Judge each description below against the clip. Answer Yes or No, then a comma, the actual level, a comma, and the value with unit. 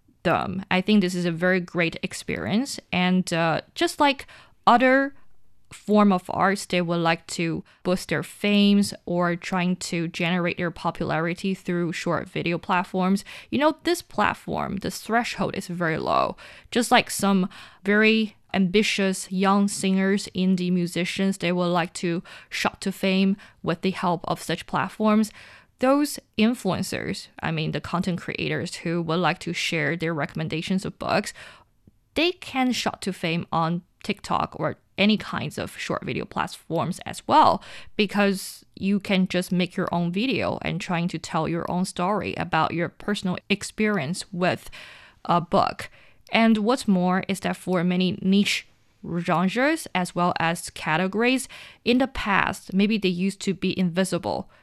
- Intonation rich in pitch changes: No, average, 2.8 semitones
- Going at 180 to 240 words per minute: No, average, 155 wpm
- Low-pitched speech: No, medium, 185 Hz